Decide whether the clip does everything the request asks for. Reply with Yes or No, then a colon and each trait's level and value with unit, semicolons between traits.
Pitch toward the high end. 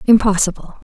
Yes: high, 205 Hz